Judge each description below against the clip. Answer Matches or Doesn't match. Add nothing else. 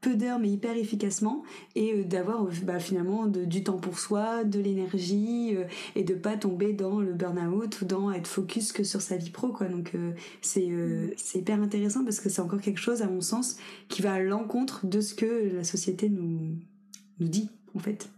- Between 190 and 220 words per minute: Matches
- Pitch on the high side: Matches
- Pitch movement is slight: Matches